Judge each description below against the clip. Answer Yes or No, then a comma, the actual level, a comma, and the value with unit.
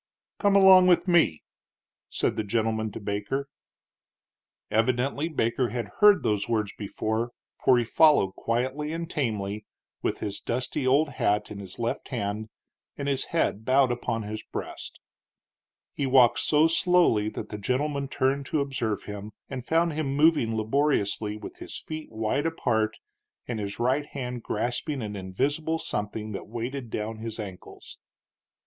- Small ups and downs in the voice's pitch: No, average, 5.1 semitones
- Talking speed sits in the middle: Yes, average, 150 wpm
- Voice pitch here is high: No, low, 120 Hz